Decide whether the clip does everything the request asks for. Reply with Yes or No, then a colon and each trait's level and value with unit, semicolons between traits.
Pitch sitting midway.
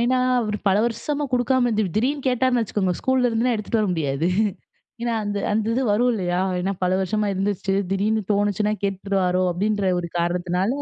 No: high, 210 Hz